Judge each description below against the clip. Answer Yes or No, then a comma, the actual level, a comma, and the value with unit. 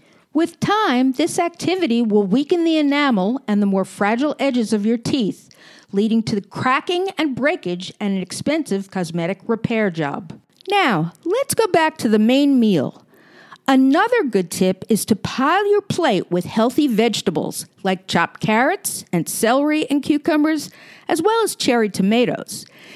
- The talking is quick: No, average, 155 wpm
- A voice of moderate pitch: No, high, 240 Hz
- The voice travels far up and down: Yes, wide, 7.7 semitones